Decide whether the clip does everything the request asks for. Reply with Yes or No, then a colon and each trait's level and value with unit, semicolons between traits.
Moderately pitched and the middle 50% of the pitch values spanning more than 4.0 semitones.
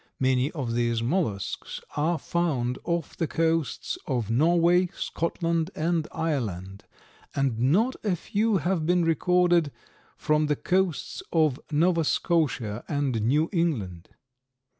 Yes: medium, 155 Hz; average, 5.3 semitones